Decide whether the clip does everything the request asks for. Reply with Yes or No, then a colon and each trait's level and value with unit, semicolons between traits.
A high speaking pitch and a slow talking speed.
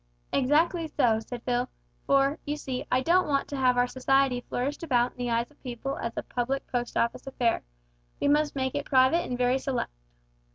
No: very high, 260 Hz; average, 200 wpm